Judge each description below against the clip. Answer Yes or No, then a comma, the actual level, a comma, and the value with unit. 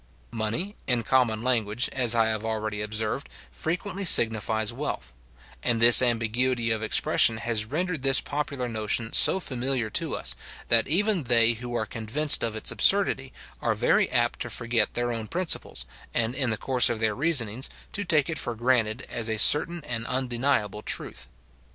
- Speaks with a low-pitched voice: Yes, low, 120 Hz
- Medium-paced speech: Yes, average, 170 wpm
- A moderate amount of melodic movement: Yes, average, 3.4 semitones